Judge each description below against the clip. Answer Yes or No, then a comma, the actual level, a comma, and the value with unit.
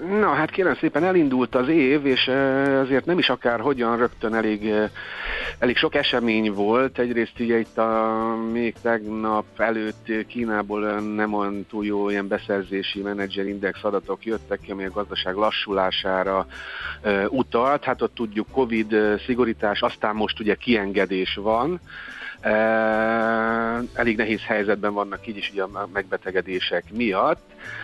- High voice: No, low, 110 Hz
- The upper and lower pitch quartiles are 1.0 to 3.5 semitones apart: Yes, average, 2.8 semitones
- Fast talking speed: No, average, 135 wpm